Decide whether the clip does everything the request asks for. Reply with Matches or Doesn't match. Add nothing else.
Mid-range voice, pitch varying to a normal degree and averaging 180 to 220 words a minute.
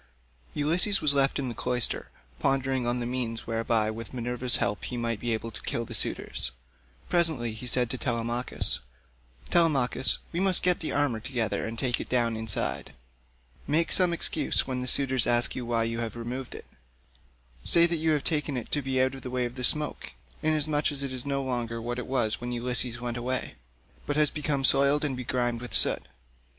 Doesn't match